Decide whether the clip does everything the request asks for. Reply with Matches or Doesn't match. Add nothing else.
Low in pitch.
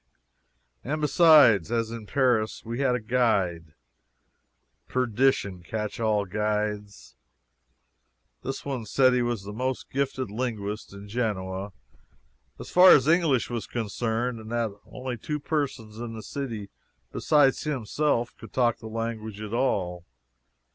Matches